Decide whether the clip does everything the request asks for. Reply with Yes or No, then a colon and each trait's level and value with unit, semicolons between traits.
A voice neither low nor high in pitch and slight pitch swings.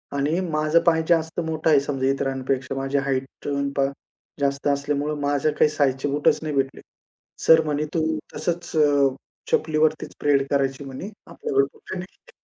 Yes: medium, 145 Hz; narrow, 2.2 semitones